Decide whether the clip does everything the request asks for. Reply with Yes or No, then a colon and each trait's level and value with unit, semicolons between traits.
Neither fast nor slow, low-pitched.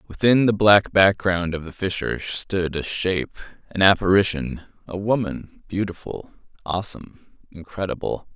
No: slow, 115 wpm; very low, 95 Hz